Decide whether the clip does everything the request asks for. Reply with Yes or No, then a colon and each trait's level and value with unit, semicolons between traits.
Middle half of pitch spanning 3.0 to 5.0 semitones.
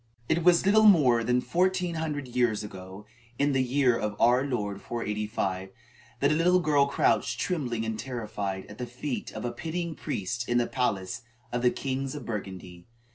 No: wide, 5.5 semitones